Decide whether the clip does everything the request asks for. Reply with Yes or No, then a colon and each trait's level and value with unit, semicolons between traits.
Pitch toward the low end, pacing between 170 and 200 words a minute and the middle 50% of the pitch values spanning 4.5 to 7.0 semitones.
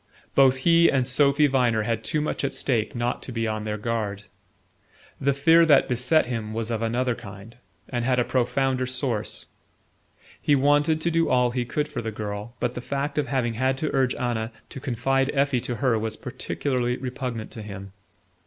No: low, 125 Hz; average, 190 wpm; average, 3.3 semitones